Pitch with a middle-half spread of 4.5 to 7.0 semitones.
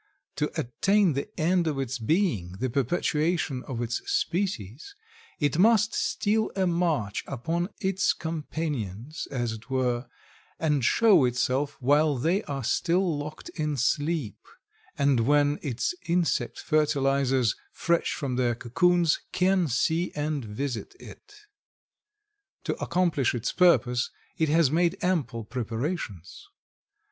Yes: wide, 5.5 semitones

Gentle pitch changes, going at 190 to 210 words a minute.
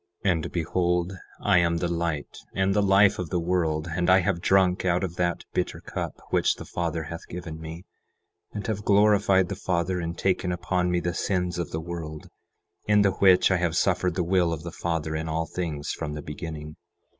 Yes: narrow, 2.2 semitones; fast, 205 wpm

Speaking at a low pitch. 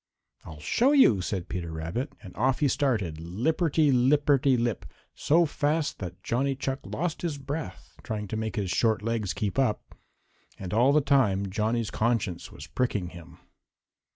Yes: low, 115 Hz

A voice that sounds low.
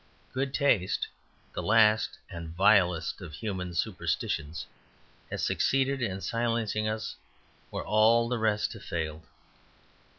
Yes: low, 110 Hz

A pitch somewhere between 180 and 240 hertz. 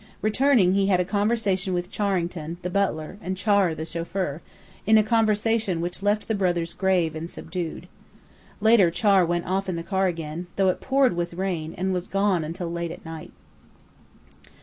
Yes: medium, 185 Hz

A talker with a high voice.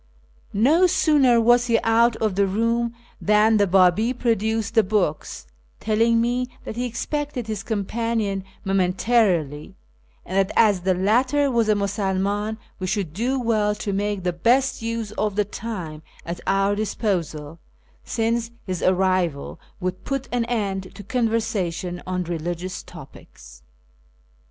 Yes: high, 210 Hz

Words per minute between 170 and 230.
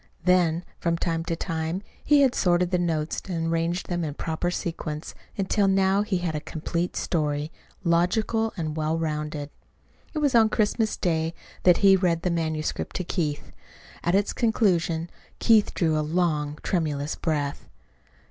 No: average, 155 wpm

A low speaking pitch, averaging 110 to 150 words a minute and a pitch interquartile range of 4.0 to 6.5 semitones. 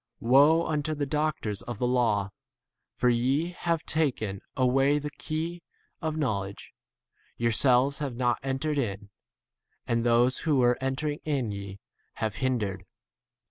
Yes: low, 130 Hz; average, 140 wpm; average, 4.3 semitones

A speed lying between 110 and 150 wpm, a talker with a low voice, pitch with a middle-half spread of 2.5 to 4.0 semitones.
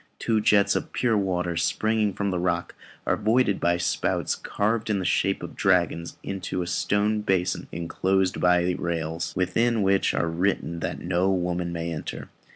No: average, 170 wpm; very low, 95 Hz; average, 2.9 semitones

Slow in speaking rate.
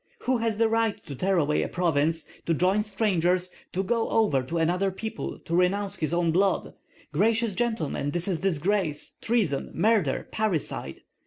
No: average, 165 wpm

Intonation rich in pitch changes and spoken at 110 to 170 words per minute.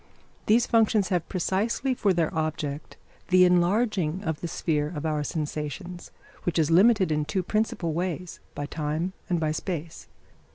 No: average, 3.4 semitones; average, 155 wpm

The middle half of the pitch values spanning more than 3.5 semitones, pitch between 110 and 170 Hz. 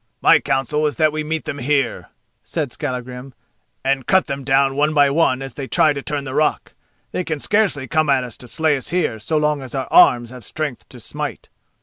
No: average, 2.8 semitones; medium, 140 Hz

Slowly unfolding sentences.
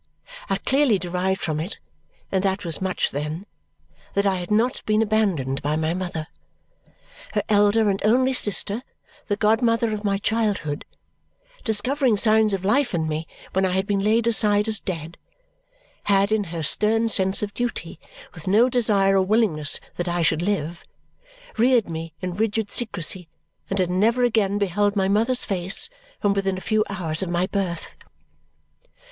No: average, 165 wpm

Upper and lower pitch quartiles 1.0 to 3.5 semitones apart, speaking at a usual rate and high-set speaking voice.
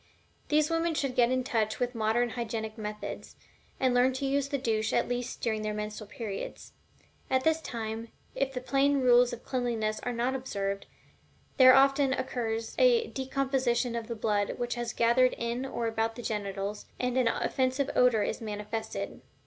Yes: average, 2.9 semitones; average, 175 wpm; high, 240 Hz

